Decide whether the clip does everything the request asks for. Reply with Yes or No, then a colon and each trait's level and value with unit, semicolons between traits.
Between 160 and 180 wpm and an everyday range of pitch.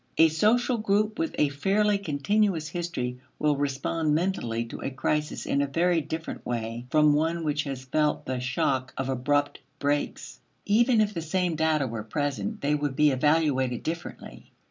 Yes: average, 165 wpm; average, 4.2 semitones